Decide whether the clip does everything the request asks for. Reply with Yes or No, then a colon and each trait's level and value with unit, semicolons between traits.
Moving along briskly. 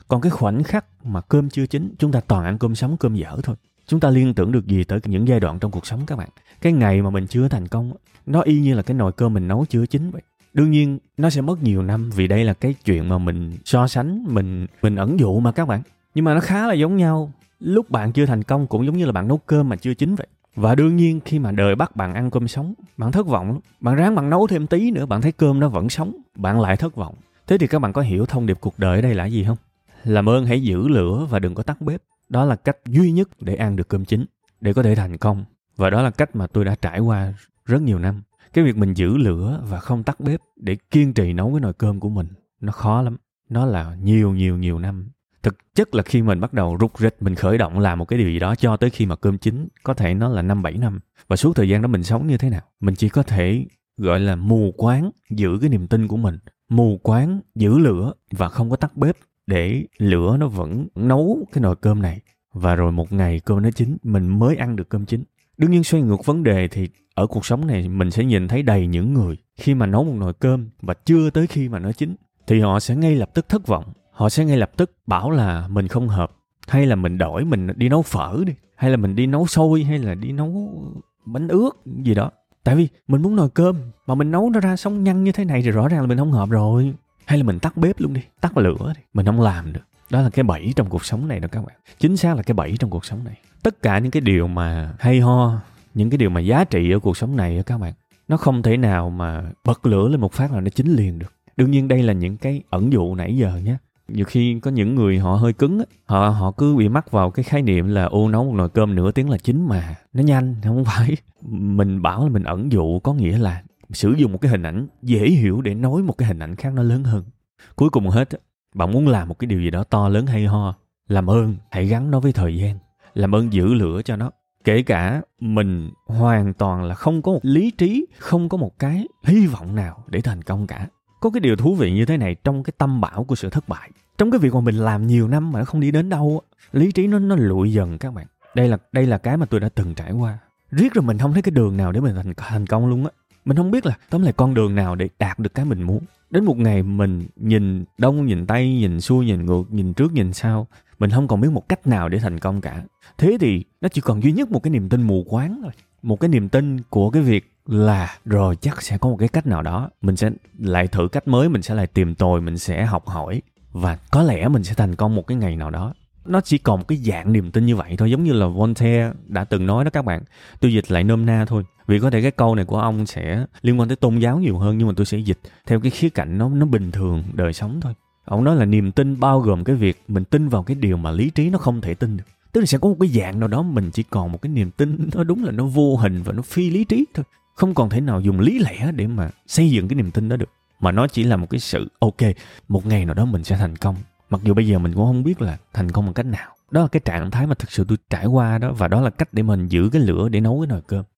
Yes: fast, 275 wpm